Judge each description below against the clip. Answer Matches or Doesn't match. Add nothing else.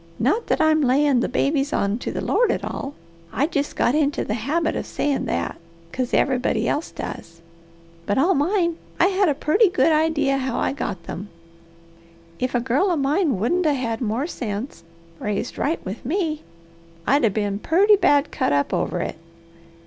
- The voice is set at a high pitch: Matches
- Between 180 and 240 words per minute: Matches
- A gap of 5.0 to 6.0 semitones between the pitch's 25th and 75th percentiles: Matches